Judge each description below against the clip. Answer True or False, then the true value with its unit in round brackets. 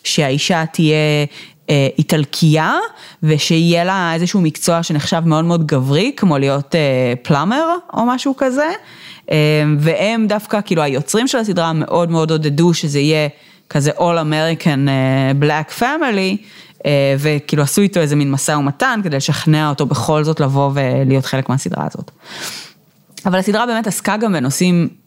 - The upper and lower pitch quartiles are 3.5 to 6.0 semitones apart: True (4.5 semitones)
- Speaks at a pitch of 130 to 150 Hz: False (160 Hz)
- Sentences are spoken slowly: False (135 wpm)